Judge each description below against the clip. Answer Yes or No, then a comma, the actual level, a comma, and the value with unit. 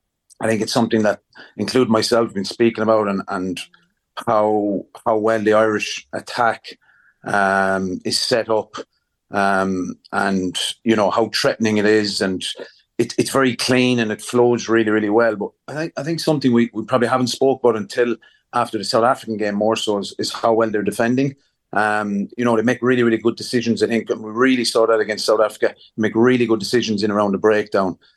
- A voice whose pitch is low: Yes, low, 110 Hz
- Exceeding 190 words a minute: Yes, average, 200 wpm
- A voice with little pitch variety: Yes, narrow, 2.3 semitones